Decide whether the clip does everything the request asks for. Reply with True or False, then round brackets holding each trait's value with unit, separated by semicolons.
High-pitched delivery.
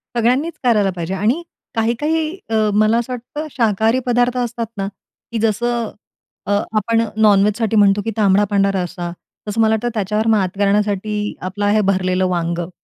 True (215 Hz)